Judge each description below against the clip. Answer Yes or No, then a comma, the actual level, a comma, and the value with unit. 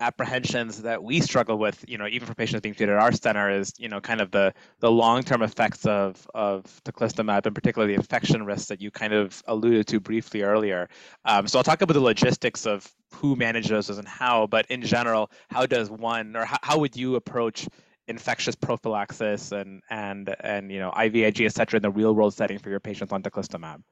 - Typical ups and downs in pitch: No, narrow, 2.2 semitones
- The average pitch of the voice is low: Yes, low, 110 Hz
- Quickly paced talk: Yes, fast, 210 wpm